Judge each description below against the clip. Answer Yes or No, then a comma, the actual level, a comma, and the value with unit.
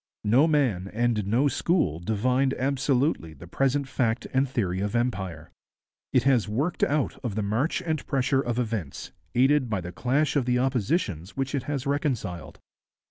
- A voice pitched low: Yes, low, 125 Hz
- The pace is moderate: Yes, average, 165 wpm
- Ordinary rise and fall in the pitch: Yes, average, 4.8 semitones